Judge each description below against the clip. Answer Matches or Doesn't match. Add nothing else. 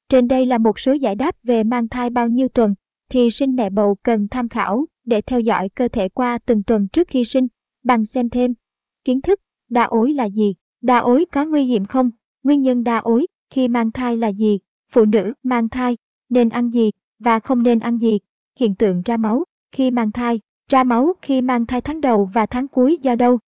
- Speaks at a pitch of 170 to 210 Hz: Doesn't match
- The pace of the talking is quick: Doesn't match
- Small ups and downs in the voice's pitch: Matches